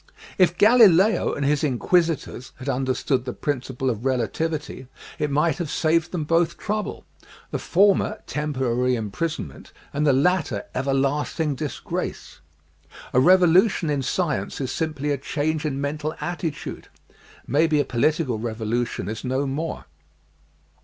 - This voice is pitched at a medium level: Yes, medium, 145 Hz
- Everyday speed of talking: No, slow, 130 wpm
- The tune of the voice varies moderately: Yes, average, 4.1 semitones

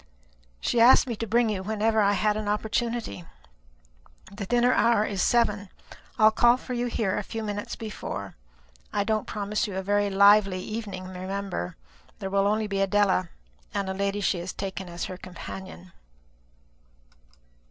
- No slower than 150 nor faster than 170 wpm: Yes, average, 165 wpm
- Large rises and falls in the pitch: No, narrow, 2.4 semitones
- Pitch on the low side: No, high, 205 Hz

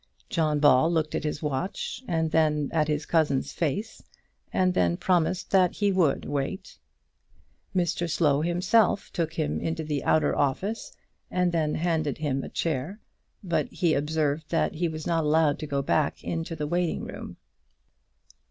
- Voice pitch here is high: No, medium, 160 Hz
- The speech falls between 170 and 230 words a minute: No, average, 160 wpm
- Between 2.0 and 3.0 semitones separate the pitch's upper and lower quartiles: Yes, average, 2.7 semitones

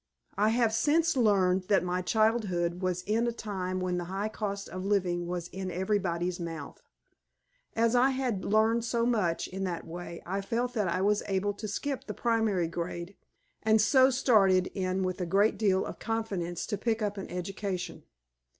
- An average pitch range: Yes, average, 3.5 semitones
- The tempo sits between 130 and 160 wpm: No, average, 180 wpm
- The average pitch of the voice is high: Yes, high, 195 Hz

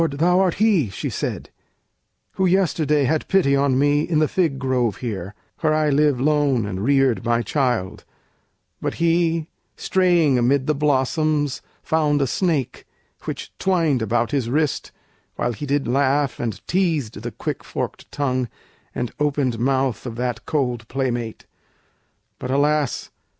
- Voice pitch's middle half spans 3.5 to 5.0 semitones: Yes, average, 3.9 semitones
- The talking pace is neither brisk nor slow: Yes, average, 145 wpm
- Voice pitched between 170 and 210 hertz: No, medium, 140 Hz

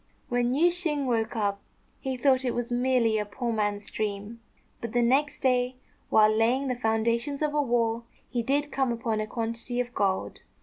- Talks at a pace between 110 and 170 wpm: No, average, 185 wpm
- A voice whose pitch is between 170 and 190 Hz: No, high, 240 Hz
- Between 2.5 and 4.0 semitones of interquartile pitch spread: Yes, average, 2.8 semitones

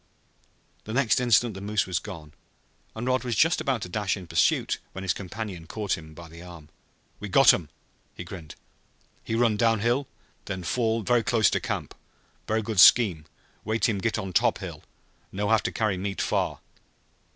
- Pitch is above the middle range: No, low, 105 Hz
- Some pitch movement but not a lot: Yes, average, 3.9 semitones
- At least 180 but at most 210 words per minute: Yes, average, 185 wpm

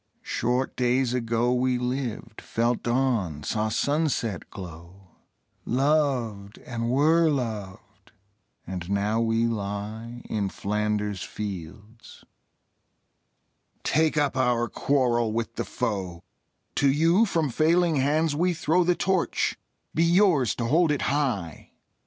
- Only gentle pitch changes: No, wide, 5.5 semitones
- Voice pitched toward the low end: Yes, low, 120 Hz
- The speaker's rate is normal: No, slow, 115 wpm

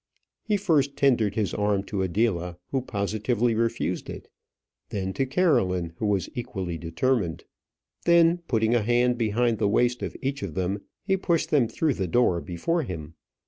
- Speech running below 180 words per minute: Yes, average, 165 wpm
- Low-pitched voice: Yes, low, 115 Hz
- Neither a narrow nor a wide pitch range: No, wide, 5.8 semitones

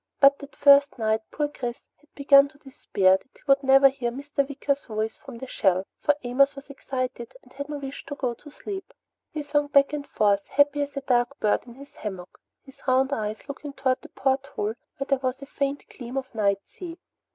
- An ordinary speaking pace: No, fast, 215 wpm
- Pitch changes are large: No, average, 2.8 semitones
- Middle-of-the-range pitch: No, very high, 275 Hz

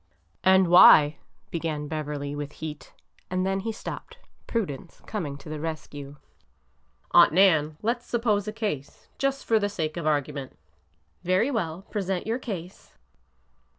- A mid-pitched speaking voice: Yes, medium, 170 Hz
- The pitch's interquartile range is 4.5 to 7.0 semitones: Yes, wide, 5.5 semitones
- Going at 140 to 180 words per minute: Yes, average, 150 wpm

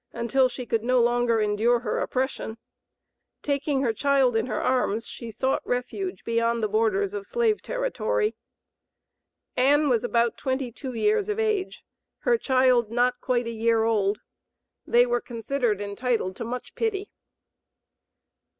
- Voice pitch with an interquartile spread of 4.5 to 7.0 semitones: No, average, 3.3 semitones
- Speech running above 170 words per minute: No, average, 145 wpm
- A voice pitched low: No, high, 245 Hz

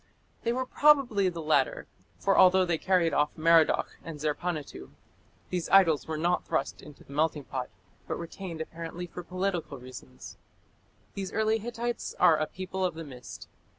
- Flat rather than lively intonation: No, average, 3.7 semitones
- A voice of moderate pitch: Yes, medium, 170 Hz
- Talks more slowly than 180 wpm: Yes, average, 160 wpm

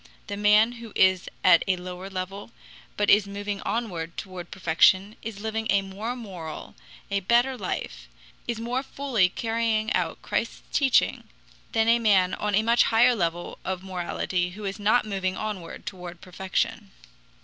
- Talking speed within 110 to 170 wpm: Yes, average, 160 wpm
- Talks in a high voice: Yes, high, 200 Hz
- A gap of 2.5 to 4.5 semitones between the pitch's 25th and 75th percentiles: Yes, average, 3.3 semitones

